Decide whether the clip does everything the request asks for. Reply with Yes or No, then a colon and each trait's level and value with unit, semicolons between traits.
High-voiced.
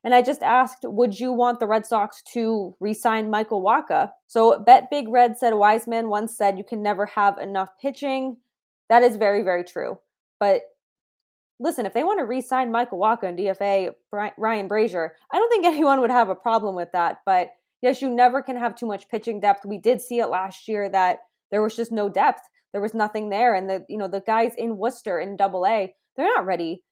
Yes: high, 220 Hz